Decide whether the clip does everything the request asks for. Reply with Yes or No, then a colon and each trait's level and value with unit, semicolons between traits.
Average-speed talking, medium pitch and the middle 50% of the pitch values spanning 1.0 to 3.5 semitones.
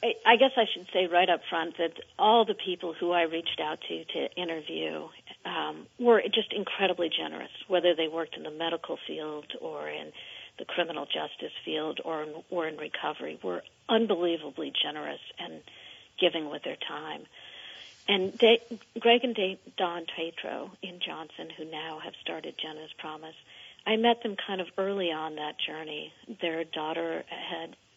No: average, 165 wpm; medium, 170 Hz; average, 4.1 semitones